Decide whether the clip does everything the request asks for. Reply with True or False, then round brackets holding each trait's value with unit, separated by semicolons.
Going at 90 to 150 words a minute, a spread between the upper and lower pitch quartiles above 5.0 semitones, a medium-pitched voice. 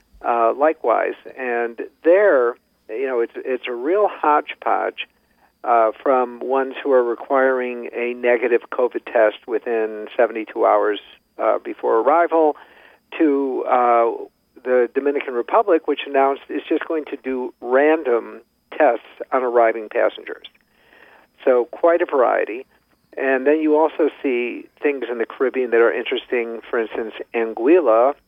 False (135 wpm; 5.4 semitones; 130 Hz)